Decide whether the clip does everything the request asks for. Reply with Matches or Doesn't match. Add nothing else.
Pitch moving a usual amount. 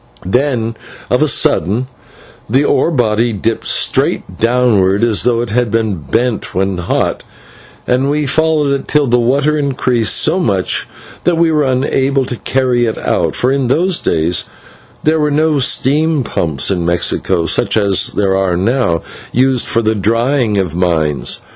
Doesn't match